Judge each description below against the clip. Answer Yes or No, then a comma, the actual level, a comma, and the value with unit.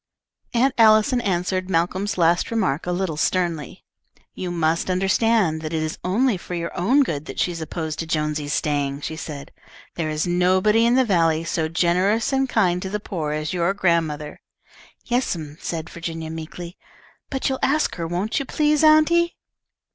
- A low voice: No, medium, 175 Hz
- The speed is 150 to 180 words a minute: Yes, average, 170 wpm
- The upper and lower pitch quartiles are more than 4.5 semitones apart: Yes, average, 5.2 semitones